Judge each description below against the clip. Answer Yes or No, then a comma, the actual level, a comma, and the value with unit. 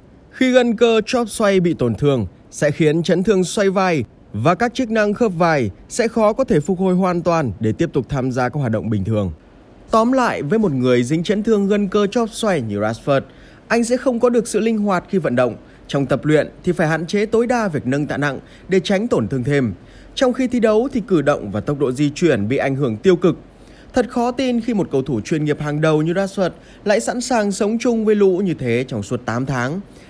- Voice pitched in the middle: Yes, medium, 175 Hz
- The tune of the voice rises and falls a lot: Yes, wide, 8.6 semitones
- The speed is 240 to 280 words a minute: Yes, average, 245 wpm